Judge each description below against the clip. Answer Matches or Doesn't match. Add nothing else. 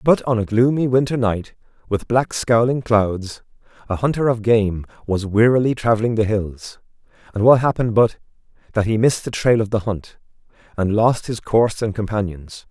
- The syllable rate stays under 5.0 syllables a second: Doesn't match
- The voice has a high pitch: Doesn't match